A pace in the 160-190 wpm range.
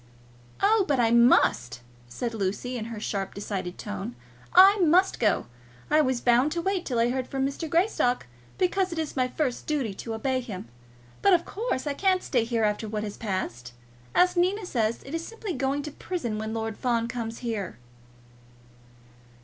Yes: average, 180 wpm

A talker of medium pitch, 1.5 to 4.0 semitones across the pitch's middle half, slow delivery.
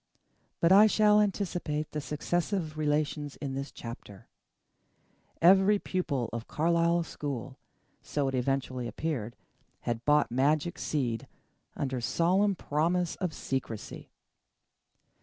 No: medium, 150 Hz; average, 4.7 semitones; slow, 110 wpm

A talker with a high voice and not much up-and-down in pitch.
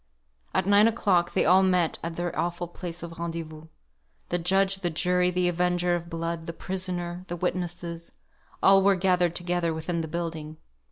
No: medium, 175 Hz; narrow, 1.3 semitones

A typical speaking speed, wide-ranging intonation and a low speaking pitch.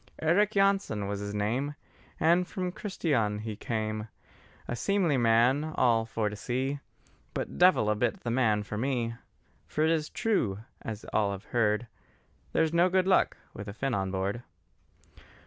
Yes: average, 165 wpm; wide, 7.4 semitones; low, 120 Hz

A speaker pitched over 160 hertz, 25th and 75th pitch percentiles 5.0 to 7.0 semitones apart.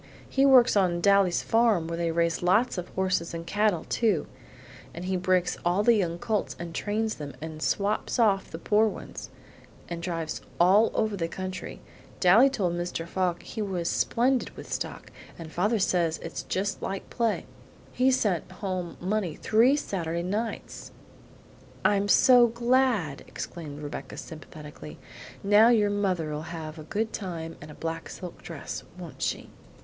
No: medium, 185 Hz; average, 4.3 semitones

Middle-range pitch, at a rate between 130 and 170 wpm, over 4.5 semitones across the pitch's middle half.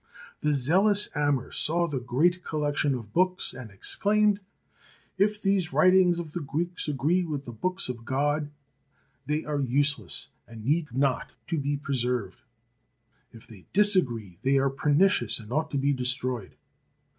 Yes: medium, 145 Hz; average, 155 wpm; wide, 5.4 semitones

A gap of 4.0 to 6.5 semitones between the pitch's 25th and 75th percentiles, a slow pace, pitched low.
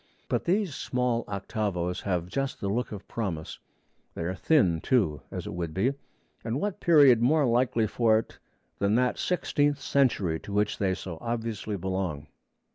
No: wide, 5.5 semitones; average, 165 wpm; low, 110 Hz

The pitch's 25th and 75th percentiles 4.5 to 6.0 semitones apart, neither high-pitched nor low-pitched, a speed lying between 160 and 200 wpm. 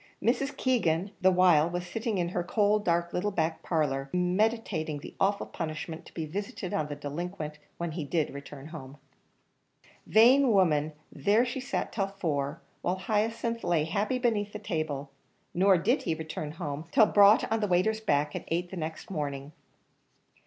Yes: average, 5.0 semitones; medium, 175 Hz; average, 170 wpm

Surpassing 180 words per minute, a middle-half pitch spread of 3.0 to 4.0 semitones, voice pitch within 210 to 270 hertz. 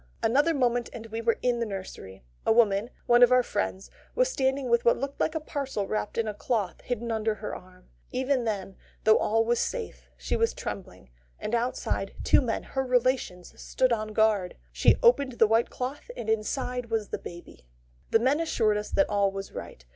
Yes: average, 200 wpm; average, 3.4 semitones; high, 230 Hz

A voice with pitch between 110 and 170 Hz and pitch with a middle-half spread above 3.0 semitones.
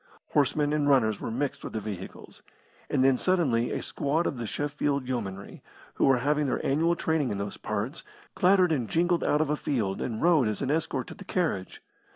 Yes: medium, 140 Hz; average, 5.3 semitones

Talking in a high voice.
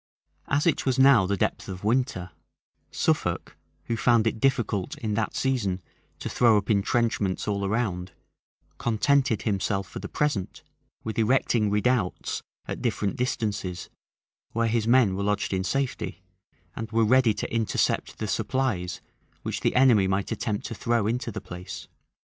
No: low, 110 Hz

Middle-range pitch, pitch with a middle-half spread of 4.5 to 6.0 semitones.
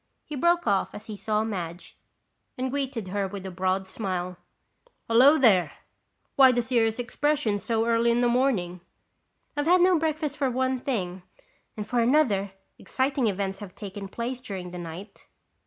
No: high, 225 Hz; average, 5.2 semitones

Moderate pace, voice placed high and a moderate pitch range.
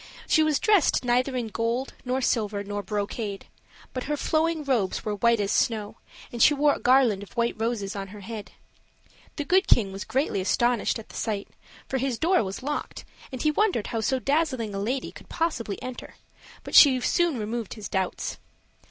Yes: average, 190 wpm; high, 240 Hz; average, 4.9 semitones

